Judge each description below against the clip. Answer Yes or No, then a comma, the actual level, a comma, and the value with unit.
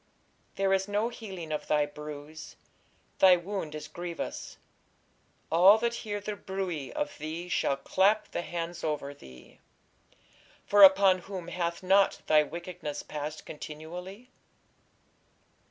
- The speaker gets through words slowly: Yes, slow, 125 wpm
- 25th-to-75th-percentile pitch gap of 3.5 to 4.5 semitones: Yes, average, 4.2 semitones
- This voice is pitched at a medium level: Yes, medium, 175 Hz